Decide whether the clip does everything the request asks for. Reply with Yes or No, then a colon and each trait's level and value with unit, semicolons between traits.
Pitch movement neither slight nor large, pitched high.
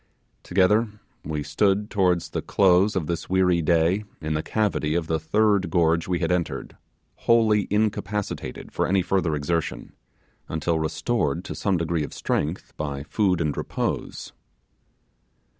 No: average, 3.8 semitones; very low, 90 Hz